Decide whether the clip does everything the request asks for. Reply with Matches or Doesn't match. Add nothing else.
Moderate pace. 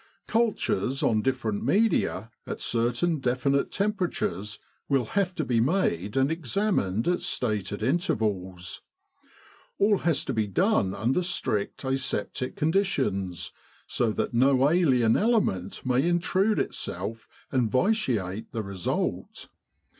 Doesn't match